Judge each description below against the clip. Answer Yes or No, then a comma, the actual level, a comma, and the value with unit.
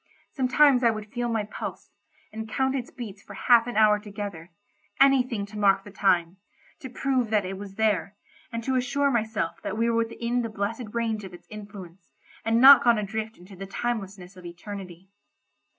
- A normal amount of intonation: Yes, average, 3.4 semitones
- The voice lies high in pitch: Yes, high, 215 Hz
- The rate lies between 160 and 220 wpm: Yes, average, 180 wpm